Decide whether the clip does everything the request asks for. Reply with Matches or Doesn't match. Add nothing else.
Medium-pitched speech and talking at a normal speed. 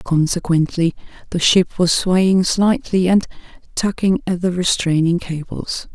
Doesn't match